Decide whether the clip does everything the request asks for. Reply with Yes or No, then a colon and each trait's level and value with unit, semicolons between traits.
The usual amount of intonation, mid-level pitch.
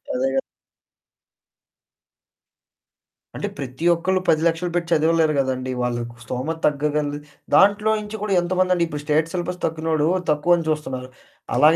Yes: average, 3.2 semitones; medium, 160 Hz